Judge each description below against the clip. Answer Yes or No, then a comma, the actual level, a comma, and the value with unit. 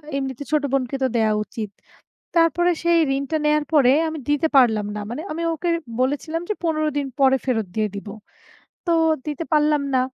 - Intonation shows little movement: No, average, 3.7 semitones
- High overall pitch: Yes, very high, 285 Hz